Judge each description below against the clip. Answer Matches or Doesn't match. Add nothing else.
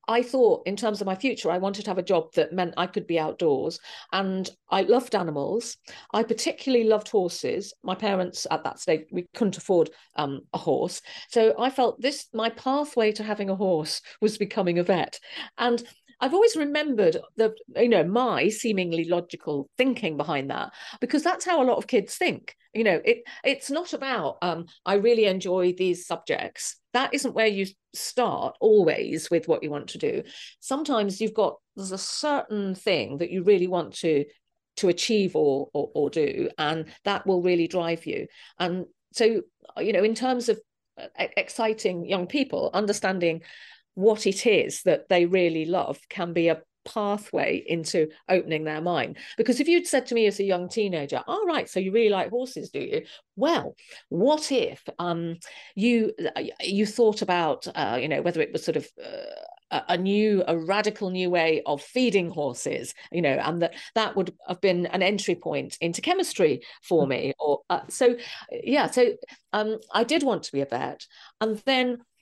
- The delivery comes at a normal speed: Matches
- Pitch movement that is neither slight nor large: Doesn't match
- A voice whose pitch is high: Matches